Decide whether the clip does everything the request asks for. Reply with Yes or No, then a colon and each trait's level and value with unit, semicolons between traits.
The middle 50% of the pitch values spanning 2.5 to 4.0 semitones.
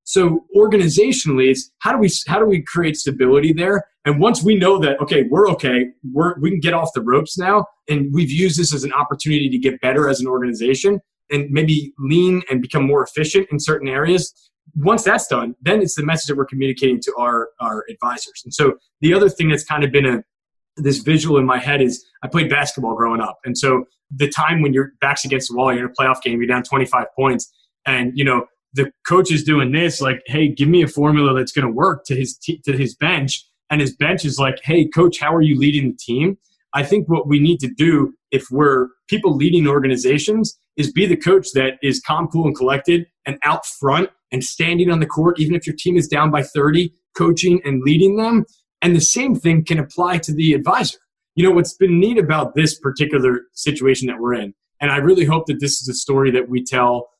No: average, 4.4 semitones